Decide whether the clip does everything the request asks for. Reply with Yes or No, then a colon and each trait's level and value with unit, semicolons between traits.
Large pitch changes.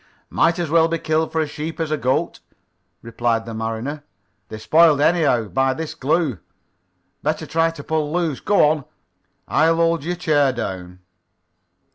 No: average, 4.0 semitones